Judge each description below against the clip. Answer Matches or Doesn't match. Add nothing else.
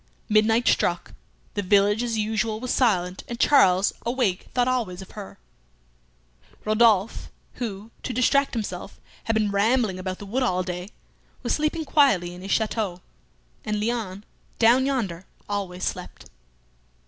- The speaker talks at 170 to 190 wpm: Doesn't match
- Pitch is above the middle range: Matches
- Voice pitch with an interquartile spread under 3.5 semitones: Doesn't match